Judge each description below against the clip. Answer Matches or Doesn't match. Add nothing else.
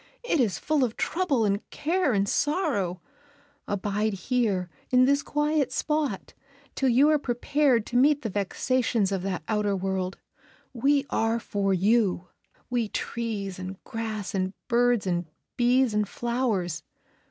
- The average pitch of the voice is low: Doesn't match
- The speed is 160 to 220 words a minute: Doesn't match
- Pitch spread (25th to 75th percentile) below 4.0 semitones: Doesn't match